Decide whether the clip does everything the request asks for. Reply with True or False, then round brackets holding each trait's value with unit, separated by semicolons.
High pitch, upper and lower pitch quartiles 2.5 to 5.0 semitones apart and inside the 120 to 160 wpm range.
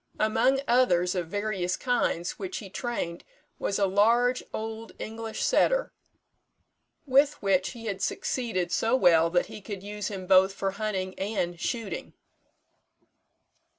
True (205 Hz; 3.5 semitones; 135 wpm)